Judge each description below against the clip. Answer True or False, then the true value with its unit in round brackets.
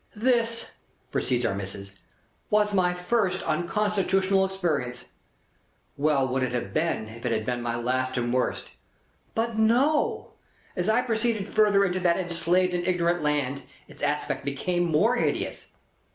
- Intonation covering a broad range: True (8.1 semitones)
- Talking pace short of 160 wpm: True (145 wpm)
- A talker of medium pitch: True (175 Hz)